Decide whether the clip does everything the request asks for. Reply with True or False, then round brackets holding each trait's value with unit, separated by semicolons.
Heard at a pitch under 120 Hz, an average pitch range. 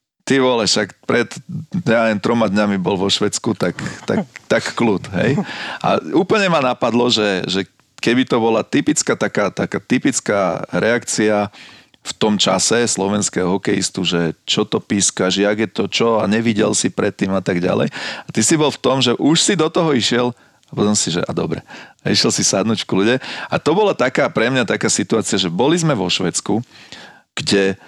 True (110 Hz; 3.8 semitones)